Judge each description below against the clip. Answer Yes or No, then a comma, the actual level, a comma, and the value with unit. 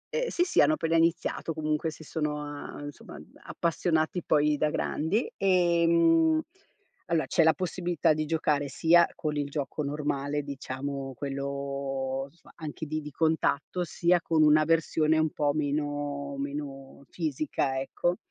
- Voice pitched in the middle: Yes, medium, 150 Hz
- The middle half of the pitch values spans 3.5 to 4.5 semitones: No, narrow, 2.5 semitones